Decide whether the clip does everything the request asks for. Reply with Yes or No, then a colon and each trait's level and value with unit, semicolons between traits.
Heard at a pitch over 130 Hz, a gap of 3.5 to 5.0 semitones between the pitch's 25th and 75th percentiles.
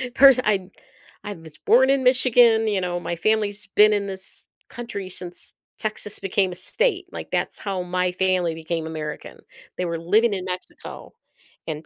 Yes: high, 190 Hz; average, 3.8 semitones